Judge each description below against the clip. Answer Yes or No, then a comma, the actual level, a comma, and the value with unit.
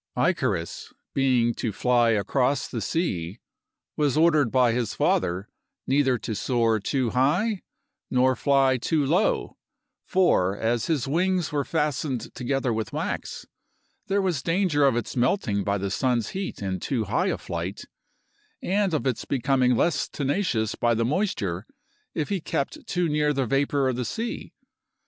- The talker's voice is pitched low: Yes, low, 130 Hz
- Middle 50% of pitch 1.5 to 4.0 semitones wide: No, average, 4.8 semitones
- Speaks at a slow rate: No, average, 155 wpm